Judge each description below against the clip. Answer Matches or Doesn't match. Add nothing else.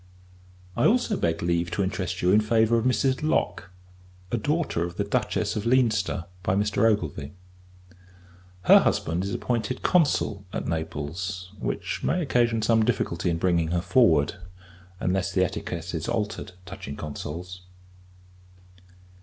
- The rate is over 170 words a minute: Doesn't match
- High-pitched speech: Doesn't match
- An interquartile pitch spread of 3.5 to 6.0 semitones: Matches